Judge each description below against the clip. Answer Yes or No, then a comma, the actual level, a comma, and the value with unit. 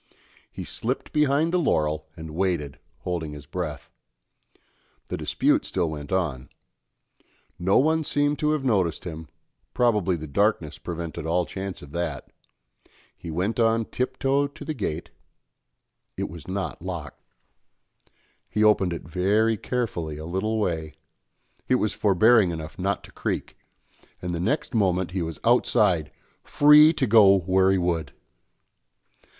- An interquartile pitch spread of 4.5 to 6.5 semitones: Yes, wide, 5.6 semitones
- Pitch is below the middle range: Yes, very low, 95 Hz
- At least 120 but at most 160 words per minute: Yes, average, 145 wpm